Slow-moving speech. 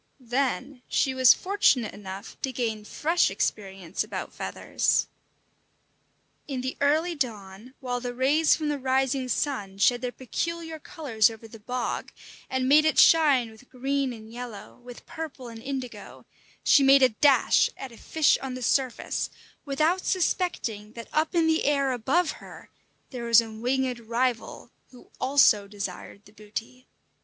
No: average, 155 wpm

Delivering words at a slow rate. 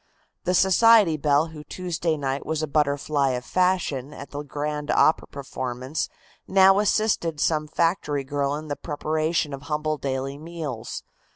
No: average, 150 wpm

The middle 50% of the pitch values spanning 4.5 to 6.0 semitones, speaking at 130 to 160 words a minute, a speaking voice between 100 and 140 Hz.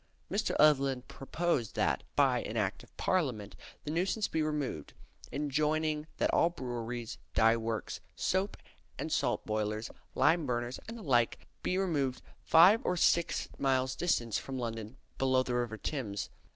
Yes: average, 5.1 semitones; average, 150 wpm; low, 135 Hz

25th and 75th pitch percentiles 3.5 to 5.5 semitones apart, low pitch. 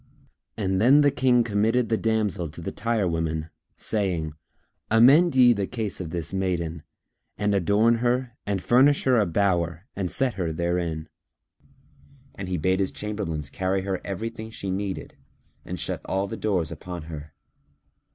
Yes: average, 4.6 semitones; low, 100 Hz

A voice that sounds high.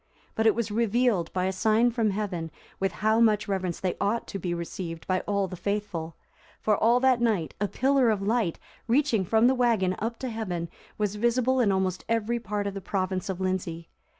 Yes: high, 205 Hz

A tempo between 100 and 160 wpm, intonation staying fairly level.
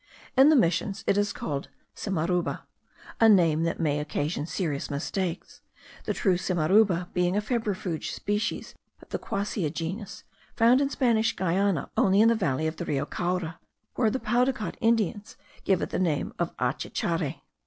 No: average, 155 wpm; average, 4.6 semitones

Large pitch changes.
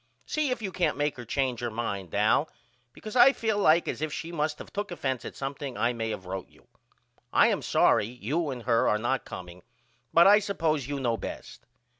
Yes: wide, 6.6 semitones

